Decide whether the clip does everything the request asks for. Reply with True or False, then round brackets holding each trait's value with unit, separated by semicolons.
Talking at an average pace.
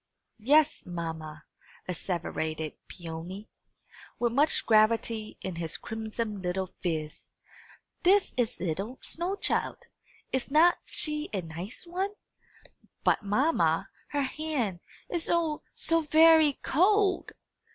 False (110 wpm)